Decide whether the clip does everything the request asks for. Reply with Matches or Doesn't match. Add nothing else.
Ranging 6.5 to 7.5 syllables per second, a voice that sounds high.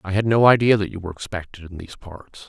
Doesn't match